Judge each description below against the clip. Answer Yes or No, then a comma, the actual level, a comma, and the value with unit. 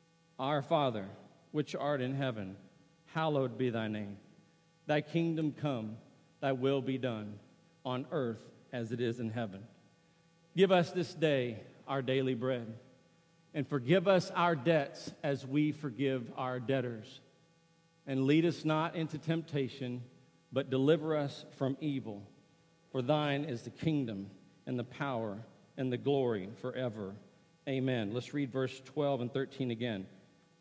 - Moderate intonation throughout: Yes, average, 4.7 semitones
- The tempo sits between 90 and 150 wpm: Yes, average, 140 wpm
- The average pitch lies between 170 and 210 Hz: No, low, 135 Hz